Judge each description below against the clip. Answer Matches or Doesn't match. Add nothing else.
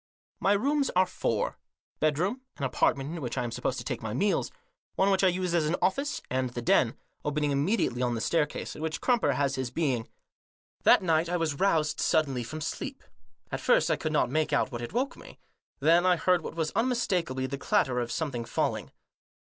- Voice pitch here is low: Doesn't match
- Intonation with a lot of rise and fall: Matches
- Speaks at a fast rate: Matches